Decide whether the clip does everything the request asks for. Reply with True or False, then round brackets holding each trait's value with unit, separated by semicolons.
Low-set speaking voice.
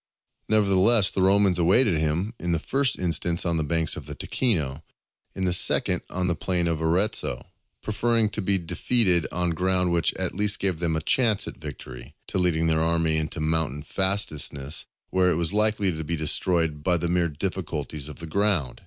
True (85 Hz)